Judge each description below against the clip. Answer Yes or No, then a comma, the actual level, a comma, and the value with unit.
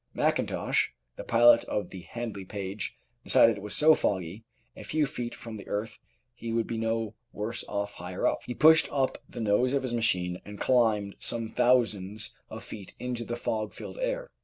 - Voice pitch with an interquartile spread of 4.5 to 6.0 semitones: No, average, 3.0 semitones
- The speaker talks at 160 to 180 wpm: No, average, 190 wpm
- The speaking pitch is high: No, low, 115 Hz